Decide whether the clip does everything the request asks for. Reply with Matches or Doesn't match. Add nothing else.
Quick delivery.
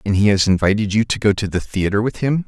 Matches